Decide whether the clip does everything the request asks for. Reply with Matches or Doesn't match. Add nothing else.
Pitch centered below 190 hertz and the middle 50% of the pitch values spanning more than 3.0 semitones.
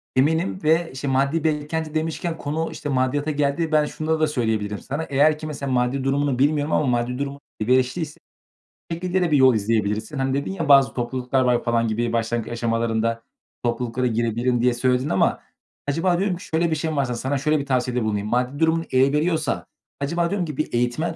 Matches